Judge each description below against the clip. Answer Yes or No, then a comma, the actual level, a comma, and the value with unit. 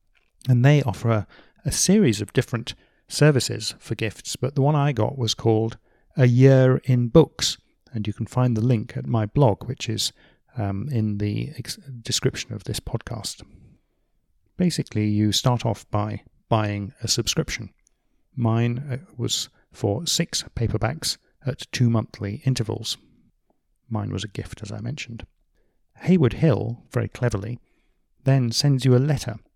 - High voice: No, low, 120 Hz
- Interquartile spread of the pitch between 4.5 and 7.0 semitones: No, average, 3.2 semitones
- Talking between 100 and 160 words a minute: Yes, average, 150 wpm